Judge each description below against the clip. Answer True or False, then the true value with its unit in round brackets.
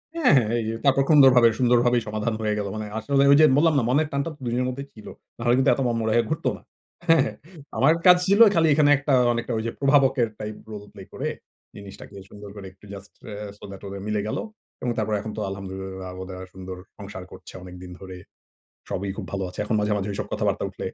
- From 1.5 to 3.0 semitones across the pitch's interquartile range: False (5.3 semitones)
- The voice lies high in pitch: False (110 Hz)